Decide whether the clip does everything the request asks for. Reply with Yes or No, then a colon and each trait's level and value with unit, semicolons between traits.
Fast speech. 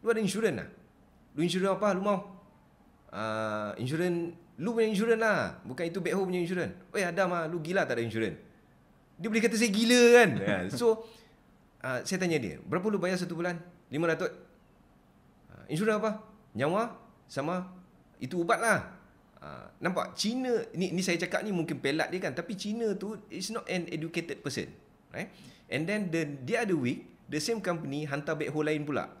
Yes: fast, 185 wpm